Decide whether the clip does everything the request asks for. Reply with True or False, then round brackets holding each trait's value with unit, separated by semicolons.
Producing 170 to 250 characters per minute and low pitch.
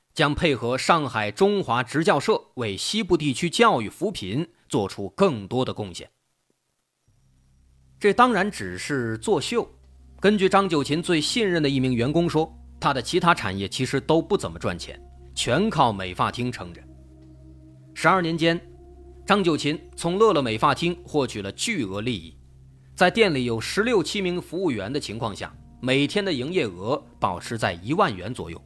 True (245 characters per minute; 130 Hz)